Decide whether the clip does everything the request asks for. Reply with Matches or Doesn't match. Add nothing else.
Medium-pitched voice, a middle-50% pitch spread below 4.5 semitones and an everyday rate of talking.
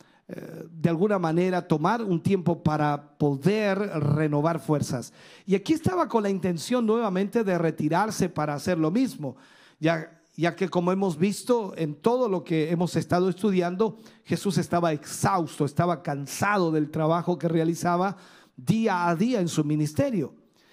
Matches